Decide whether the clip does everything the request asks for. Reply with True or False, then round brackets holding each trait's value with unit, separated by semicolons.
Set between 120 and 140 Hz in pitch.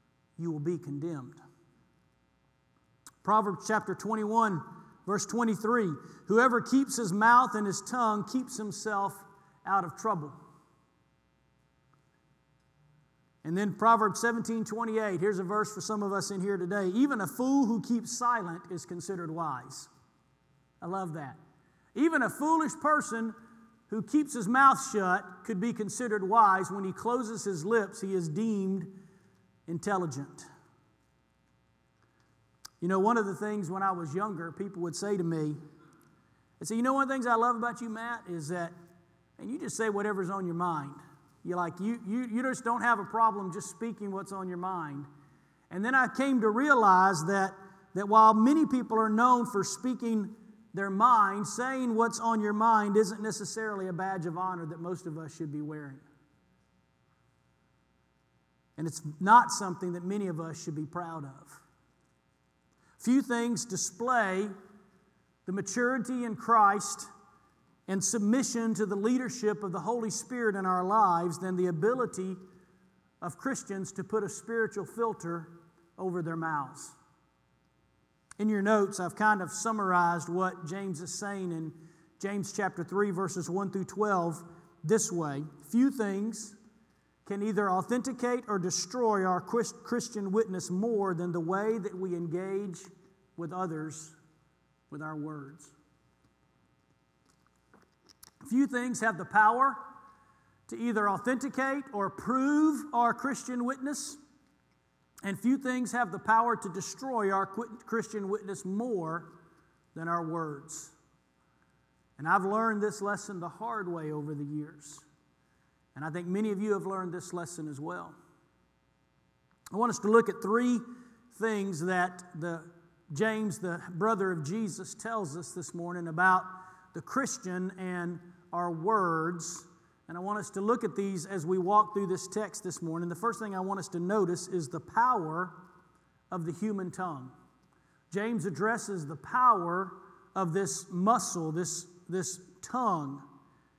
False (190 Hz)